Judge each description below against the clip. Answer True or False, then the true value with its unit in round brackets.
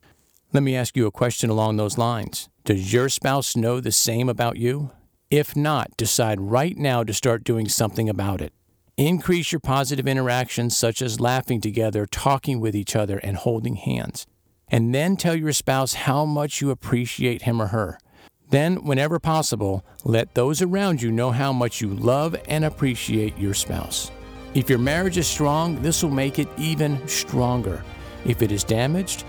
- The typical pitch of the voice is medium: False (125 Hz)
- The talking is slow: False (175 wpm)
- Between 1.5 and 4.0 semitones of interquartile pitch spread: False (4.5 semitones)